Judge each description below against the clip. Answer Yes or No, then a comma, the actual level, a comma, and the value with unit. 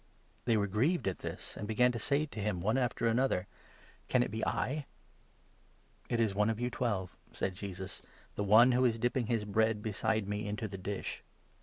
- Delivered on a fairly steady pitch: No, average, 3.2 semitones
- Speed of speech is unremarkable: No, fast, 215 wpm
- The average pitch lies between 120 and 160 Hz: No, low, 110 Hz